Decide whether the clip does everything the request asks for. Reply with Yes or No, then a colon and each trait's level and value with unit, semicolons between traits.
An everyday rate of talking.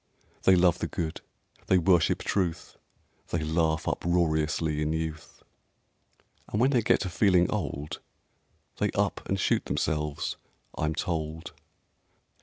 No: slow, 125 wpm